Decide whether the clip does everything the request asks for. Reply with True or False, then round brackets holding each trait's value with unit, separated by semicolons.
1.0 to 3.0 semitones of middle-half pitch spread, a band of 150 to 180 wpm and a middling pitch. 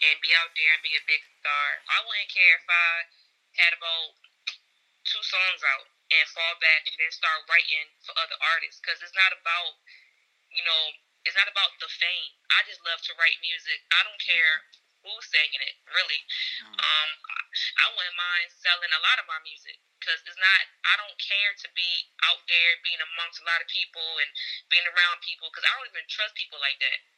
False (2.6 semitones; 200 wpm; 170 Hz)